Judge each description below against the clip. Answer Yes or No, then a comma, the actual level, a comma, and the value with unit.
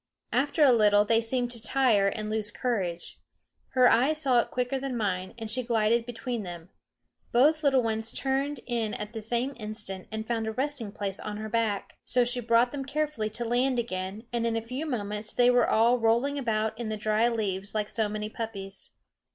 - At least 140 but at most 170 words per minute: No, average, 200 wpm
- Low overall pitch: No, high, 230 Hz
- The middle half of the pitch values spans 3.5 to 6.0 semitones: No, average, 2.7 semitones